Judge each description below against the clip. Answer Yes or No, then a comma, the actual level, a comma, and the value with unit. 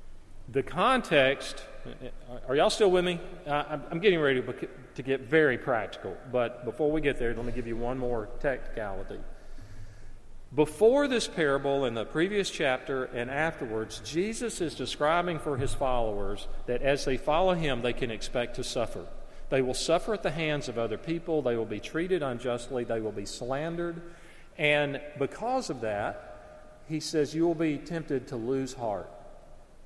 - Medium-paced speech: Yes, average, 165 wpm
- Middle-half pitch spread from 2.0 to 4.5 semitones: No, average, 5.1 semitones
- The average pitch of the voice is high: No, low, 135 Hz